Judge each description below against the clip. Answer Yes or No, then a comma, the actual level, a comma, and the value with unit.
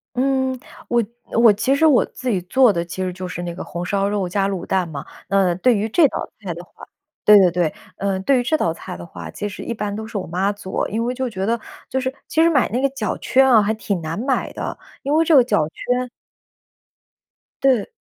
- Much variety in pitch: Yes, wide, 5.7 semitones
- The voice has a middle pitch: No, high, 210 Hz